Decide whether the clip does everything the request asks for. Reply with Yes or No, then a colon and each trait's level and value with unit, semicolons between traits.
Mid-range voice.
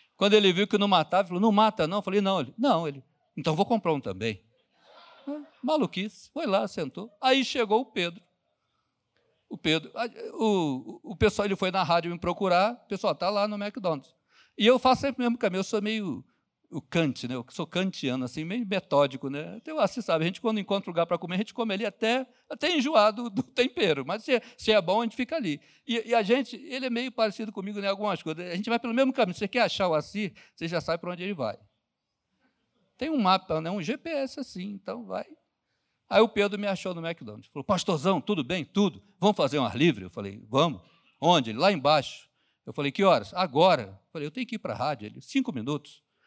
No: high, 200 Hz